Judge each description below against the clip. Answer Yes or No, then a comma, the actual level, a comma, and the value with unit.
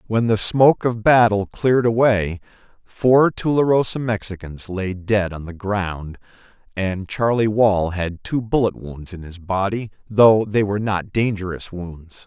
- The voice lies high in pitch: No, low, 105 Hz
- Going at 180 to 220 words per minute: No, average, 150 wpm